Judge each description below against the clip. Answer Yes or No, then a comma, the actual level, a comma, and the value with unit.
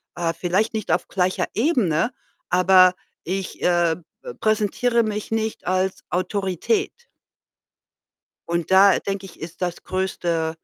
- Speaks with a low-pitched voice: No, high, 190 Hz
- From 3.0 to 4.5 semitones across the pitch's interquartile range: Yes, average, 3.5 semitones